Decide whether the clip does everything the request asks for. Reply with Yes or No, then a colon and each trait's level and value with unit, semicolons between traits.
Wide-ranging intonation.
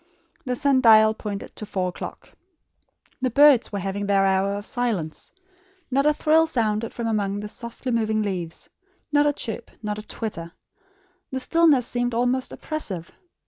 No: average, 4.1 semitones